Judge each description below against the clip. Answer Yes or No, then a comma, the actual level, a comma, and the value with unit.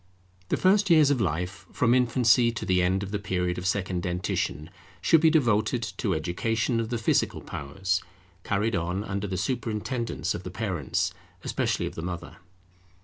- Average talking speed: Yes, average, 170 wpm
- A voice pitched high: No, low, 100 Hz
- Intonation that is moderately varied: Yes, average, 4.6 semitones